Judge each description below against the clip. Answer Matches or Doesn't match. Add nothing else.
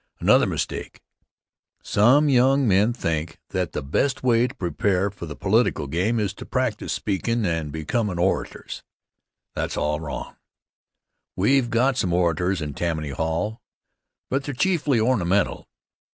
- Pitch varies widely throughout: Matches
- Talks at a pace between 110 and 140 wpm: Matches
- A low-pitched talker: Matches